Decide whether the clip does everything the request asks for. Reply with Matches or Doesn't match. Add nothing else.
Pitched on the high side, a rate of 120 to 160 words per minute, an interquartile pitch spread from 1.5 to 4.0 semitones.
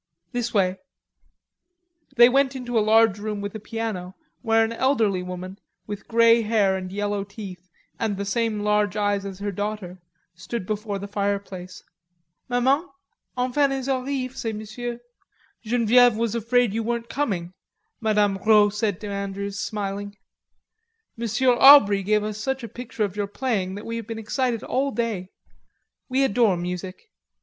Matches